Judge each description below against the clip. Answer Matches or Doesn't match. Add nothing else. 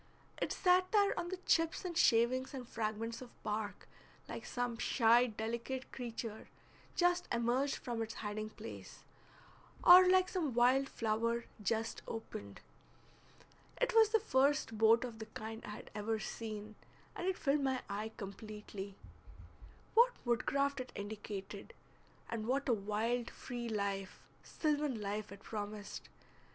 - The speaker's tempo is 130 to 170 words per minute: Matches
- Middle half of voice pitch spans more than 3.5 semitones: Matches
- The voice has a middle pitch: Doesn't match